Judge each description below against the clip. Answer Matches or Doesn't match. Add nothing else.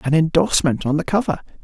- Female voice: Doesn't match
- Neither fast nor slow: Matches